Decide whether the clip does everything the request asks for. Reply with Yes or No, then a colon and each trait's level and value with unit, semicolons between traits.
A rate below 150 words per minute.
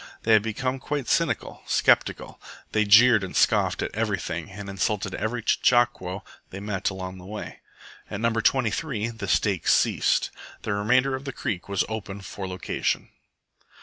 No: average, 155 wpm